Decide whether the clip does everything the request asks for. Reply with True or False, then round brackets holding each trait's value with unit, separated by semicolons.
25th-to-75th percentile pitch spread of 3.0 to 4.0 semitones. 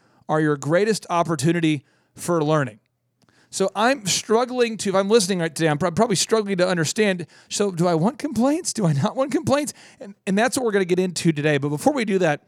False (5.4 semitones)